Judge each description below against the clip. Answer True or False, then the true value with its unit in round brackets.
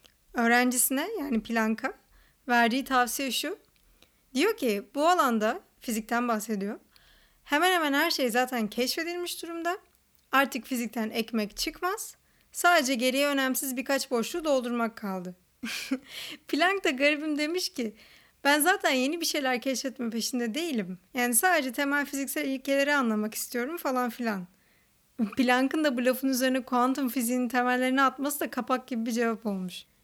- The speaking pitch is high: True (260 Hz)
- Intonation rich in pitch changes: False (3.8 semitones)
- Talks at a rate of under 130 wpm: False (135 wpm)